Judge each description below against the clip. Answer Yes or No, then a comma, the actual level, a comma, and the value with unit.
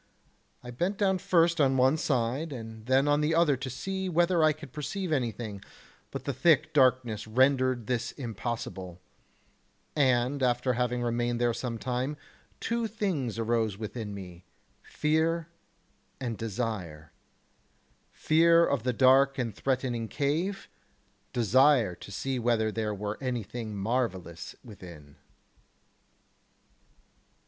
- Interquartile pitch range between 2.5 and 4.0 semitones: No, average, 4.6 semitones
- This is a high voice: No, low, 125 Hz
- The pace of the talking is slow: Yes, slow, 125 wpm